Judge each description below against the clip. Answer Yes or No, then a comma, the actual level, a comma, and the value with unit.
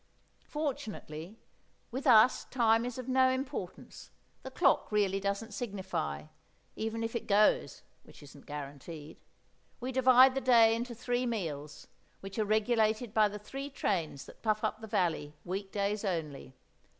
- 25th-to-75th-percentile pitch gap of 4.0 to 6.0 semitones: Yes, average, 4.8 semitones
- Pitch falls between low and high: No, high, 215 Hz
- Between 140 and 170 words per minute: Yes, average, 150 wpm